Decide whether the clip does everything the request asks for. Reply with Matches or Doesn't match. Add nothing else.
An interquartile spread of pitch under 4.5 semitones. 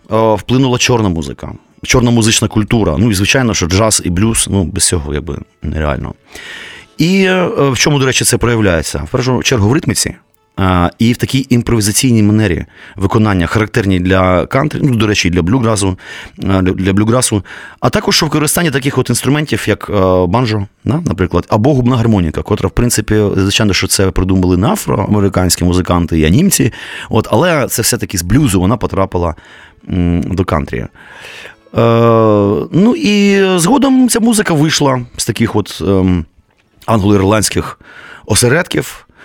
Doesn't match